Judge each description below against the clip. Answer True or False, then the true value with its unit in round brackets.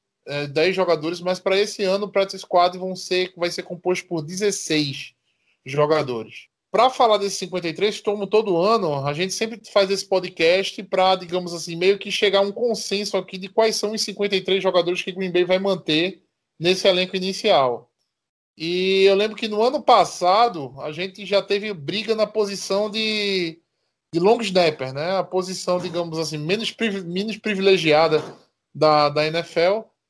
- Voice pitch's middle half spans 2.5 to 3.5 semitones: True (2.9 semitones)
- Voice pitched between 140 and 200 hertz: True (190 Hz)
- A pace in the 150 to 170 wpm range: True (165 wpm)